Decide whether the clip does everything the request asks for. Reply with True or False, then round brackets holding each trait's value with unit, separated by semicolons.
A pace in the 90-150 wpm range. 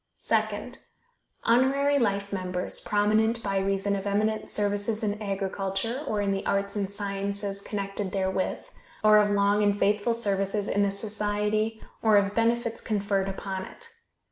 True (145 wpm)